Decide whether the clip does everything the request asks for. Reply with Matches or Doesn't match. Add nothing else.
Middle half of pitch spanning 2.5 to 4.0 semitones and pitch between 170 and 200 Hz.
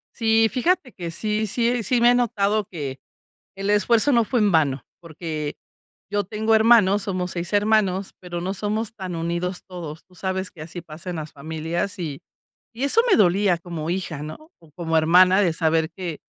Doesn't match